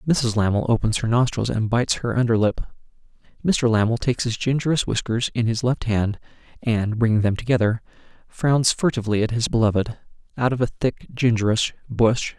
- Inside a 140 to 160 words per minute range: No, average, 170 wpm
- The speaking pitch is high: No, low, 115 Hz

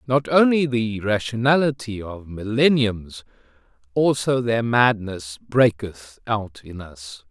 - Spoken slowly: Yes, slow, 100 wpm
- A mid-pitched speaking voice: No, low, 110 Hz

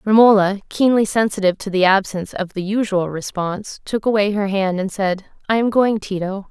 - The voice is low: No, high, 200 Hz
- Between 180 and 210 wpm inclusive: Yes, average, 185 wpm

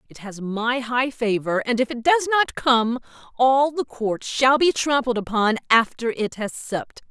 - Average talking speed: Yes, average, 185 wpm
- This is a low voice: No, high, 245 Hz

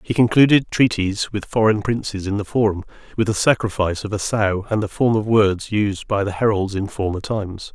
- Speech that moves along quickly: Yes, fast, 210 wpm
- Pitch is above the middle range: No, low, 105 Hz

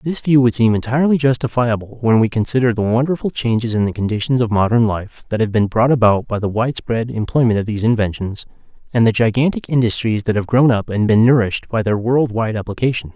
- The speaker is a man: Yes, male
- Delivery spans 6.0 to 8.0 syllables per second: Yes, 6.1 syllables/s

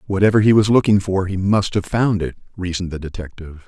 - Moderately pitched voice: No, very low, 95 Hz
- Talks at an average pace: No, fast, 210 wpm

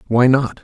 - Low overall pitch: Yes, low, 125 Hz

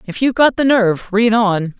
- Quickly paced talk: Yes, fast, 235 wpm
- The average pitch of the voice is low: No, high, 220 Hz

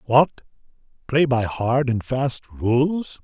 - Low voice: Yes, low, 130 Hz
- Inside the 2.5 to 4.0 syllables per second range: Yes, 2.9 syllables/s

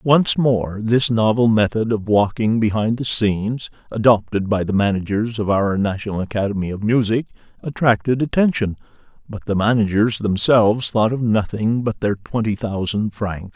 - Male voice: Yes, male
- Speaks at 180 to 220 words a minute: No, average, 150 wpm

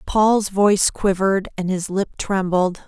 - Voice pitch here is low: No, high, 195 Hz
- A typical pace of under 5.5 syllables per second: Yes, 4.3 syllables/s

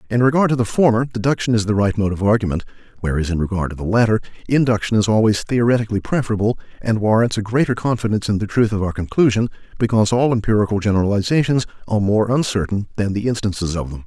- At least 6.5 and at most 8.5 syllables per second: Yes, 7.0 syllables/s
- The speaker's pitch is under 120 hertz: Yes, low, 110 Hz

